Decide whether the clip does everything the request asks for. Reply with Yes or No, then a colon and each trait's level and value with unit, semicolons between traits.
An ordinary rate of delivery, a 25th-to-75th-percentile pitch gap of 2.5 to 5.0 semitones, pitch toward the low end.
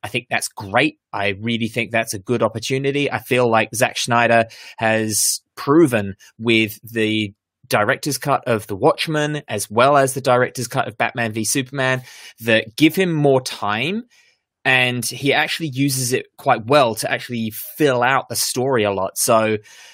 Yes: average, 170 wpm; average, 3.6 semitones; low, 120 Hz